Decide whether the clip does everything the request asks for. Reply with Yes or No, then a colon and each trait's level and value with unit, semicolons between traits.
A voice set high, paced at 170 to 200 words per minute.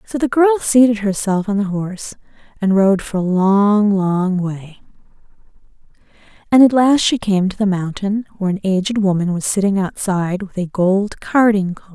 Yes: high, 200 Hz; average, 175 wpm